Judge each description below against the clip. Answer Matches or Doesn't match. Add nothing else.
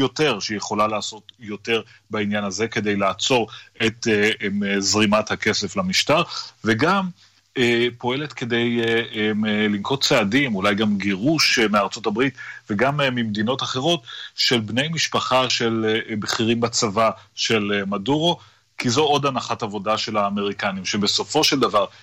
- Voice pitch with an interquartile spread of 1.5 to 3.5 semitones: Matches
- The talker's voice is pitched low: Matches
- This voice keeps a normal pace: Matches